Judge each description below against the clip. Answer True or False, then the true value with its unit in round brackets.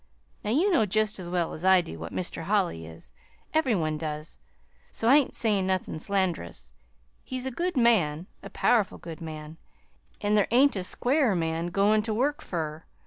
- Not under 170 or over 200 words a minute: True (185 wpm)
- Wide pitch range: True (6.0 semitones)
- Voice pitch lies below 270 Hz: True (190 Hz)